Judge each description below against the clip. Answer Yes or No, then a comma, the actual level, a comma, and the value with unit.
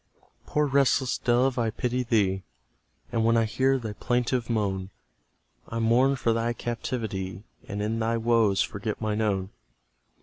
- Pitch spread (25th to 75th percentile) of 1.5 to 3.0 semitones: Yes, narrow, 2.6 semitones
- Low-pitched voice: Yes, low, 115 Hz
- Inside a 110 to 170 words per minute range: Yes, average, 145 wpm